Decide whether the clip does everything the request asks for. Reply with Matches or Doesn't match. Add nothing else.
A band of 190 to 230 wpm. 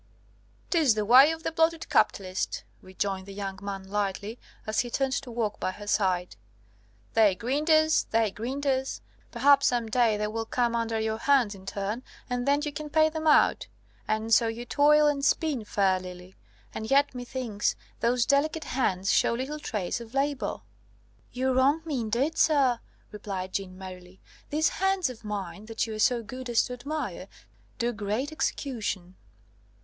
Doesn't match